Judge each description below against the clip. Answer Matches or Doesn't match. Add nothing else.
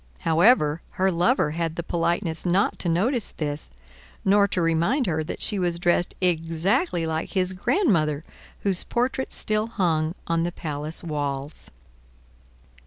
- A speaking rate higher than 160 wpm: Doesn't match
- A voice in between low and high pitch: Matches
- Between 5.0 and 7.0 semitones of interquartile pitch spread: Doesn't match